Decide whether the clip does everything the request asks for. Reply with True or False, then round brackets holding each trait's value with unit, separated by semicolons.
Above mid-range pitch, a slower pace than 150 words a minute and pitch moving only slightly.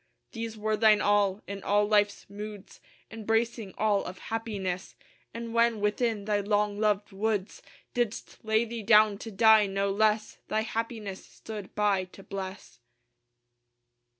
True (210 Hz; 140 wpm; 1.7 semitones)